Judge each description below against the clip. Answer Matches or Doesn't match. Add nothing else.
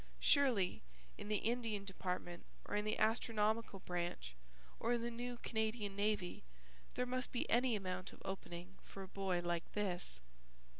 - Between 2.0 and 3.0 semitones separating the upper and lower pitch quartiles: Doesn't match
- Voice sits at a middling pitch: Doesn't match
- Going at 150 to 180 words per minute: Matches